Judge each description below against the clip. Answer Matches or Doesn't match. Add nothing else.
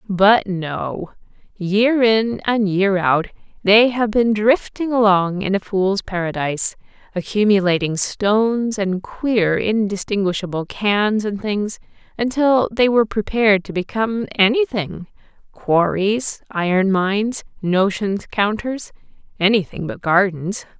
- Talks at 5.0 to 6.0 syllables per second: Doesn't match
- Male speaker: Doesn't match